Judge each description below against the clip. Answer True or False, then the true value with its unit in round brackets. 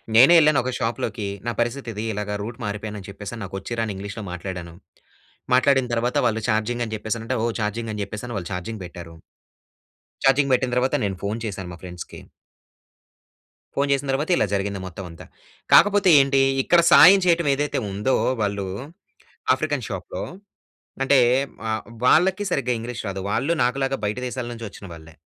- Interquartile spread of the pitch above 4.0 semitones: True (4.9 semitones)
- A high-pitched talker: False (115 Hz)